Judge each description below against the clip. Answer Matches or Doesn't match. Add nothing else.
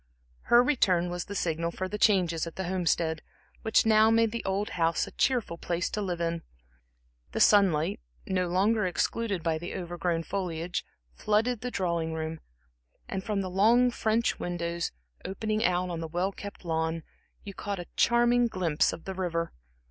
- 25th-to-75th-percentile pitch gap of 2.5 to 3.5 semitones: Doesn't match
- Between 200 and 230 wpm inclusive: Doesn't match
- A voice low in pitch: Doesn't match